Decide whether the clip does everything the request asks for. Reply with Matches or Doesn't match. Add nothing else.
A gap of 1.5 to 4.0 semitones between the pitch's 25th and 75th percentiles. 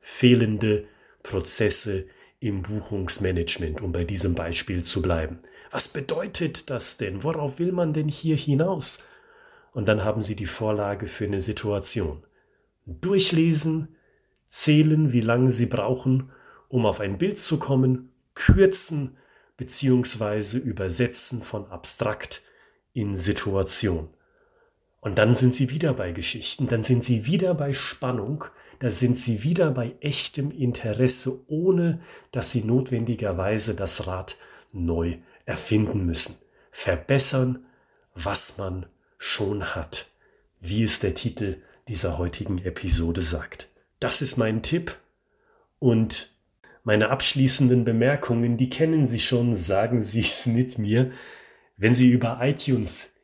Doesn't match